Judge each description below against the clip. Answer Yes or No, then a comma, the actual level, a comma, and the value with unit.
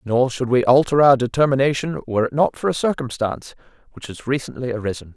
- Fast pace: No, average, 185 wpm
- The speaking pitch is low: Yes, low, 130 Hz